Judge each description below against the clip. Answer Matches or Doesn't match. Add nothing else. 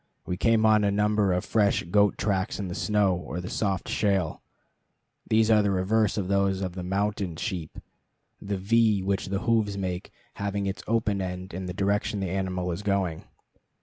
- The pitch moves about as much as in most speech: Doesn't match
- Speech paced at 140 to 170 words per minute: Doesn't match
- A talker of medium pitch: Doesn't match